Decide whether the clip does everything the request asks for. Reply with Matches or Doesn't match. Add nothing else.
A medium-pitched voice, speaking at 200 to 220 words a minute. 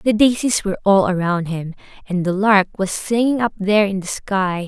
Doesn't match